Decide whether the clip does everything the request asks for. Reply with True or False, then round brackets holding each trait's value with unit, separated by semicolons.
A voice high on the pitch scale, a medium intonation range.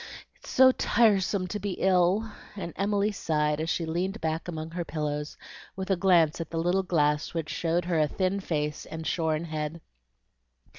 False (170 Hz; 3.4 semitones)